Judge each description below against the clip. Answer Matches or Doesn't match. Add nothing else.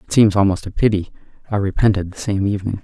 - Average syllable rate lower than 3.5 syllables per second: Doesn't match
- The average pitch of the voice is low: Matches